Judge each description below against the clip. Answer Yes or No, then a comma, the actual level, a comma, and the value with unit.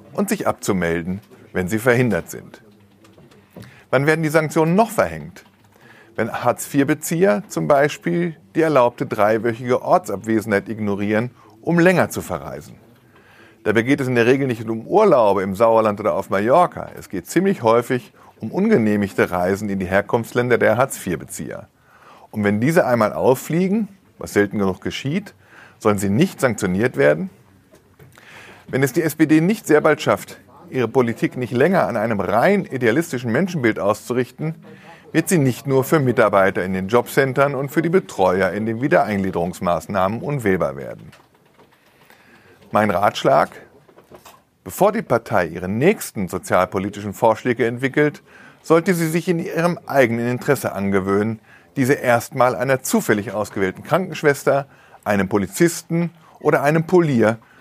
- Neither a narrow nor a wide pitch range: No, wide, 7.1 semitones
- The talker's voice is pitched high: No, low, 125 Hz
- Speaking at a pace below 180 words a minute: Yes, average, 135 wpm